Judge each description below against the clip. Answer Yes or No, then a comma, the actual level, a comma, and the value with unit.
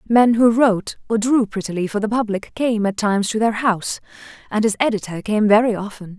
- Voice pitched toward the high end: Yes, high, 215 Hz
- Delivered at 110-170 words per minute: No, fast, 205 wpm